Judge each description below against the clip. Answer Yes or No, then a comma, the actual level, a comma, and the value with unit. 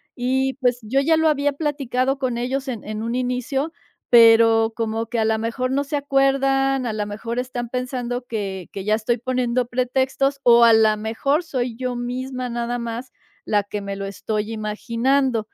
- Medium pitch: No, high, 245 Hz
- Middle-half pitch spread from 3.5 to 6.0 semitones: No, average, 2.9 semitones